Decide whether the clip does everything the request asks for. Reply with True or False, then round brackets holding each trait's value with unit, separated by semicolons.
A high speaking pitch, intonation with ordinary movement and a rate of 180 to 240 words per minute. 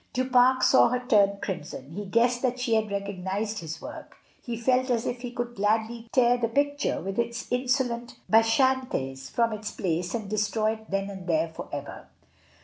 True (225 Hz; 3.8 semitones; 185 wpm)